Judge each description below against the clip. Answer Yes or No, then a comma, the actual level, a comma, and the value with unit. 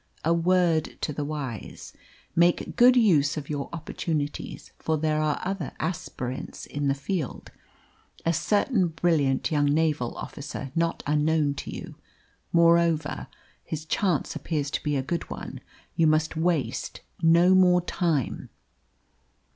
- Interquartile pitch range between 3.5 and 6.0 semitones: No, average, 2.8 semitones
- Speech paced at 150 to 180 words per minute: No, slow, 135 wpm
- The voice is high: No, medium, 160 Hz